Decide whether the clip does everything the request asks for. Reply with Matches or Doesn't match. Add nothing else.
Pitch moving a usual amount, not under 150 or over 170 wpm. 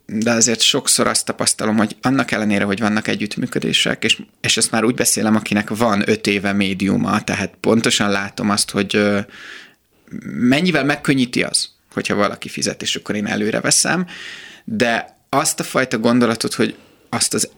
Matches